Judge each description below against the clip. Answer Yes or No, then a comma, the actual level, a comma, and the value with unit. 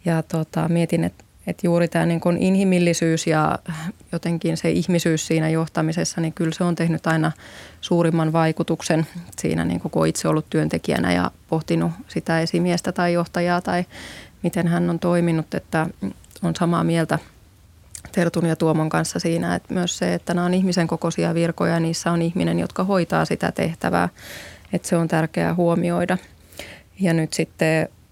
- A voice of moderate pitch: Yes, medium, 165 Hz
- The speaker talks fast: Yes, fast, 160 wpm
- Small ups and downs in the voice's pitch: Yes, narrow, 1.6 semitones